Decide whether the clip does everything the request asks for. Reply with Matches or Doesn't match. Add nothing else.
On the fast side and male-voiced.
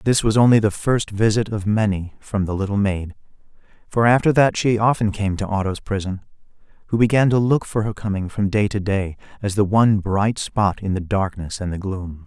Matches